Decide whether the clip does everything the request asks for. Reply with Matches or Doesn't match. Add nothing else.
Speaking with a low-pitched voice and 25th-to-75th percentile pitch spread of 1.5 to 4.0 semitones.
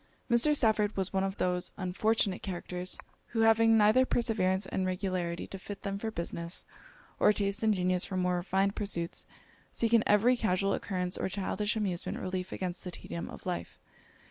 Doesn't match